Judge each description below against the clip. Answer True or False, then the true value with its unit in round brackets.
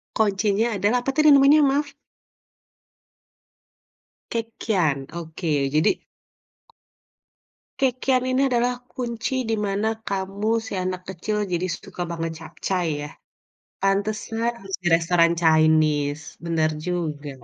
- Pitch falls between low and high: False (195 Hz)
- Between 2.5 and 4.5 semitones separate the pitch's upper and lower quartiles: False (5.6 semitones)